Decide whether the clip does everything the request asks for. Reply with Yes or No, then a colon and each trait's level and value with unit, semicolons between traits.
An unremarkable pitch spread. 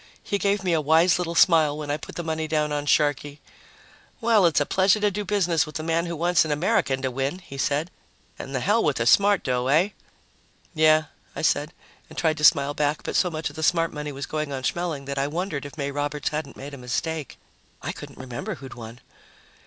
Yes: average, 3.2 semitones